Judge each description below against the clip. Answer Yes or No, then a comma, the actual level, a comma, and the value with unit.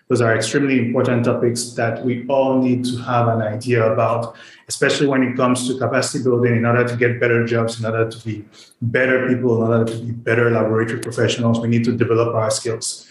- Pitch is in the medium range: No, low, 120 Hz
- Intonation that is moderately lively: No, narrow, 1.6 semitones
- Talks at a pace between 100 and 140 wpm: No, fast, 210 wpm